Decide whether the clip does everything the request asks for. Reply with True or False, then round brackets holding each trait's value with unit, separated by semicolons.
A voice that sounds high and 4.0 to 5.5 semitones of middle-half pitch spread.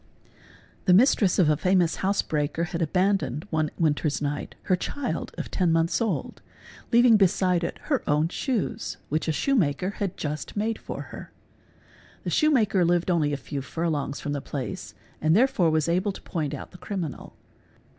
False (175 Hz; 4.5 semitones)